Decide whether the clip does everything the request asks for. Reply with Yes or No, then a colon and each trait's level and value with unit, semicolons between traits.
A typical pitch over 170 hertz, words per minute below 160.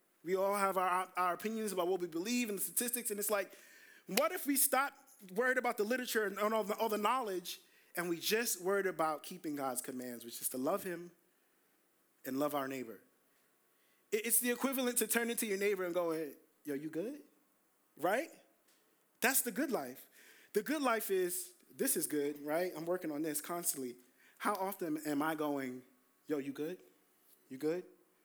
No: high, 190 Hz; average, 190 wpm